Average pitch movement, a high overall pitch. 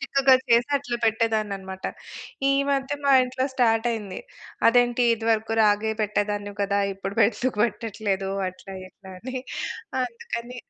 Yes: average, 3.1 semitones; high, 225 Hz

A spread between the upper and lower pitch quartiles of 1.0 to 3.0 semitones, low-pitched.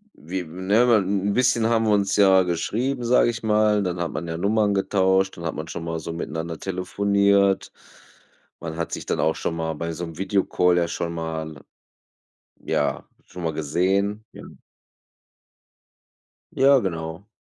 No: average, 3.7 semitones; very low, 95 Hz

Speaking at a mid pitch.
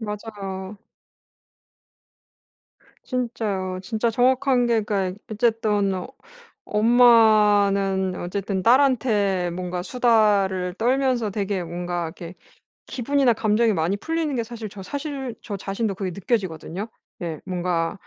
No: high, 205 Hz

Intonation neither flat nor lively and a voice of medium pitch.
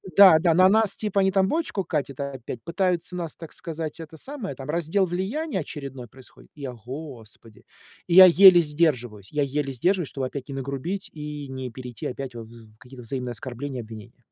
No: wide, 6.1 semitones; medium, 150 Hz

